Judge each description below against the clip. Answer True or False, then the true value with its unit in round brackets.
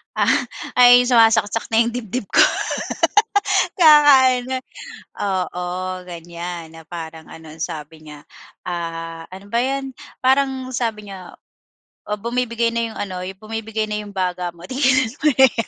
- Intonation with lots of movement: True (6.1 semitones)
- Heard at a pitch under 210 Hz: False (215 Hz)